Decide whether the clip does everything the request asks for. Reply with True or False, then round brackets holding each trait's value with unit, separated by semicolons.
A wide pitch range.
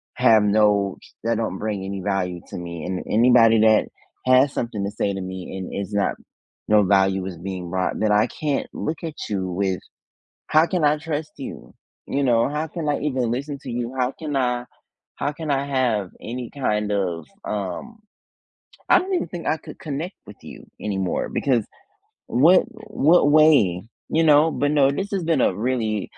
True (6.7 semitones)